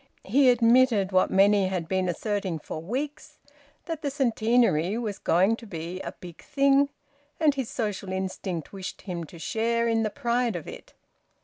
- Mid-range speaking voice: No, high, 215 Hz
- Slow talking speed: No, average, 170 wpm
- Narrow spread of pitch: No, average, 4.9 semitones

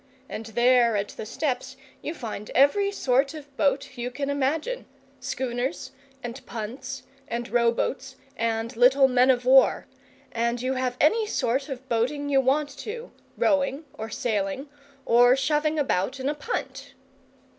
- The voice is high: Yes, very high, 260 Hz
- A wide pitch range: No, average, 3.0 semitones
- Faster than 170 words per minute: No, average, 150 wpm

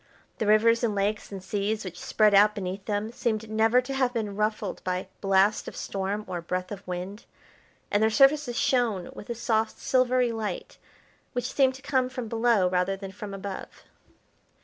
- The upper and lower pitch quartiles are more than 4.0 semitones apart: No, average, 3.2 semitones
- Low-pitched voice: No, high, 215 Hz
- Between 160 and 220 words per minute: Yes, average, 180 wpm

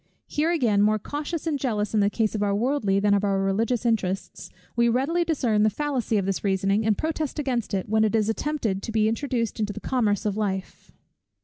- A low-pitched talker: No, high, 220 Hz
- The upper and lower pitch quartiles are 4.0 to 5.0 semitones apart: Yes, average, 4.3 semitones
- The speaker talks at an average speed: No, fast, 215 wpm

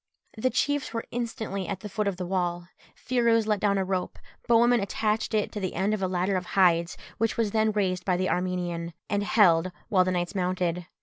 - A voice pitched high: Yes, high, 195 Hz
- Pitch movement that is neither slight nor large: Yes, average, 3.1 semitones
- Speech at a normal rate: No, fast, 210 wpm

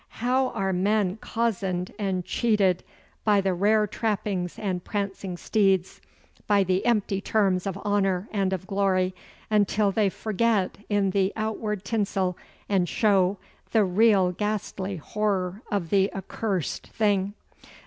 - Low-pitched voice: No, high, 195 Hz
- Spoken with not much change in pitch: Yes, narrow, 2.1 semitones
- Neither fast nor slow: No, slow, 130 wpm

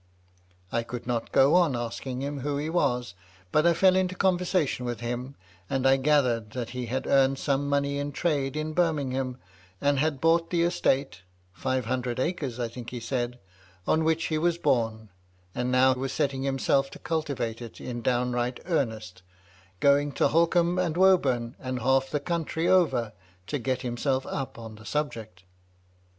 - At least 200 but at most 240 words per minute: No, average, 170 wpm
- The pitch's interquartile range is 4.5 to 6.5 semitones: No, average, 3.9 semitones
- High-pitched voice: No, low, 135 Hz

